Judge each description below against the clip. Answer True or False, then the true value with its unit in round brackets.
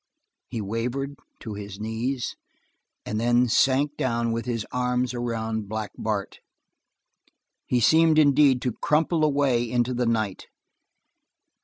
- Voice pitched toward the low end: True (120 Hz)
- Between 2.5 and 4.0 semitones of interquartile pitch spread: True (3.2 semitones)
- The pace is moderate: False (125 wpm)